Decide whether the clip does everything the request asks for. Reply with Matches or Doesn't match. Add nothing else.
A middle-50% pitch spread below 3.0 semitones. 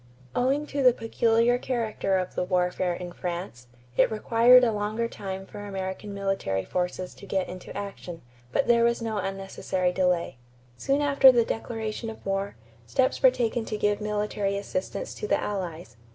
Doesn't match